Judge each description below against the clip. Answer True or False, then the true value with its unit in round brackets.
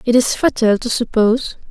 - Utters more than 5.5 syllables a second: False (5.4 syllables/s)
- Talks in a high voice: True (235 Hz)